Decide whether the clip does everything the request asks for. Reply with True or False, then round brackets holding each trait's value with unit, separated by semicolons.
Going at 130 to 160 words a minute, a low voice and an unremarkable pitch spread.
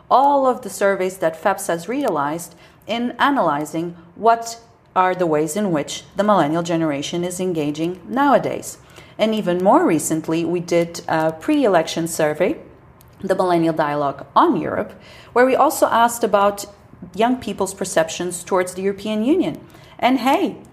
False (145 wpm; 185 Hz; 4.7 semitones)